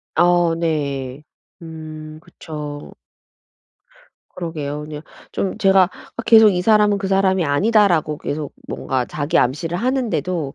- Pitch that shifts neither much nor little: Yes, average, 4.5 semitones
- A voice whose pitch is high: No, medium, 165 Hz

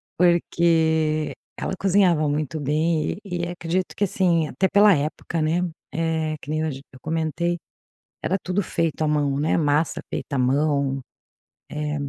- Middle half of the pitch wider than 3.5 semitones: No, narrow, 2.4 semitones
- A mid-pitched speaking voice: Yes, medium, 160 Hz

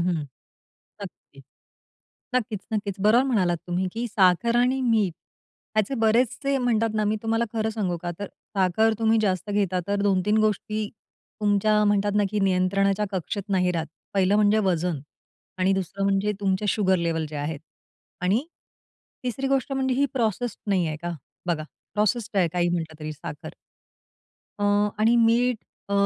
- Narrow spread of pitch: No, average, 3.5 semitones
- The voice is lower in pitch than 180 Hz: No, high, 205 Hz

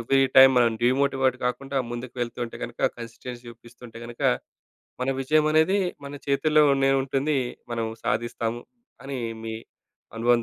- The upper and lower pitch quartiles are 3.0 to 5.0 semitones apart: No, narrow, 2.6 semitones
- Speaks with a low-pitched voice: Yes, low, 130 Hz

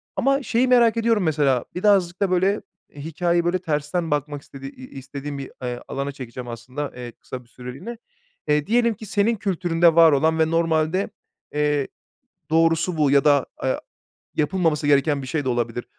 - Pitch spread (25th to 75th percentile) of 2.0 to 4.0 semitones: No, average, 4.7 semitones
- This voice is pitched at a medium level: Yes, medium, 155 Hz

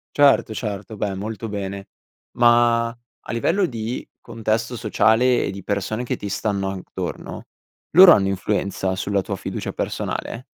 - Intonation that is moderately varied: Yes, average, 3.1 semitones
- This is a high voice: No, low, 110 Hz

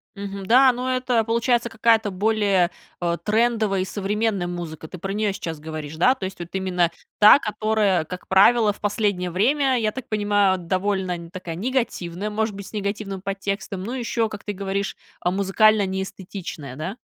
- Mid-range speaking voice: No, high, 200 Hz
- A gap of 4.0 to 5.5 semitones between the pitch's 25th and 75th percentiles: No, average, 2.9 semitones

